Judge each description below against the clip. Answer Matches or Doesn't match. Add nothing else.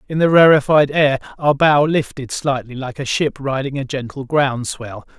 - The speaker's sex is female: Doesn't match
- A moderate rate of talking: Matches